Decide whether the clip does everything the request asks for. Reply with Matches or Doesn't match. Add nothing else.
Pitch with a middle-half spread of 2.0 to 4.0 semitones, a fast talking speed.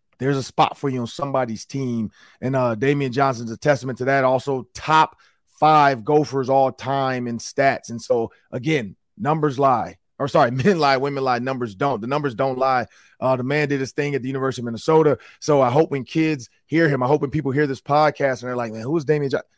Matches